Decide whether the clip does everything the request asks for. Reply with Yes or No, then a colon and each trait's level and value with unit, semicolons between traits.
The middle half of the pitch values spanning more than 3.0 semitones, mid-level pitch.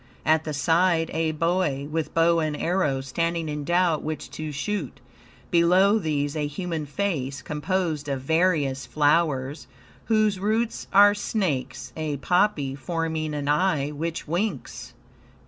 Yes: average, 3.5 semitones; medium, 160 Hz